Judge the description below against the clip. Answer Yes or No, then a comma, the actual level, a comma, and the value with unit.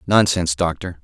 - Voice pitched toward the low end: Yes, very low, 90 Hz